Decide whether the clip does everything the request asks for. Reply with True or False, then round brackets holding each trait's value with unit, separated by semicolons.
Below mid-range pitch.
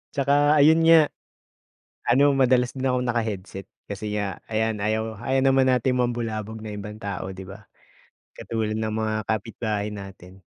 True (110 Hz)